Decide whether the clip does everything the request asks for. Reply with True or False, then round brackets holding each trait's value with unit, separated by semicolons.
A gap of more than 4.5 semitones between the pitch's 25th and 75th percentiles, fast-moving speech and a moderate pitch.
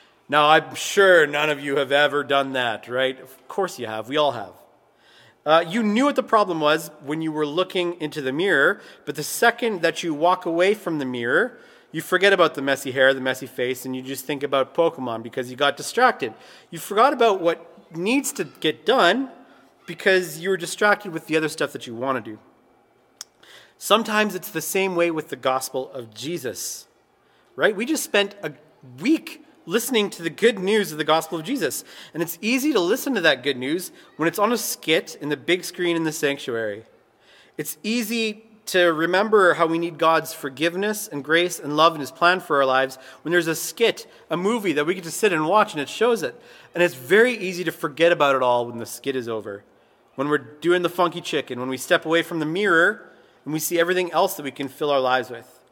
True (5.3 semitones; 220 wpm; 165 Hz)